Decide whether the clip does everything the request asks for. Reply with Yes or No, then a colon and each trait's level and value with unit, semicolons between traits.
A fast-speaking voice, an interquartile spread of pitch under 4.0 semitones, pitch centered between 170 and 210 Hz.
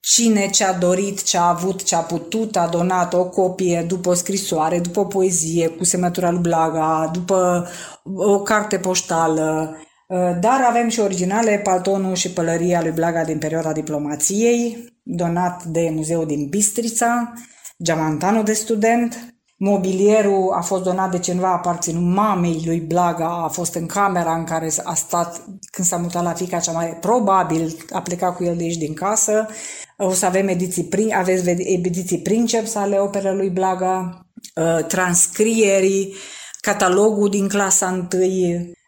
No: average, 155 wpm; average, 2.8 semitones; medium, 185 Hz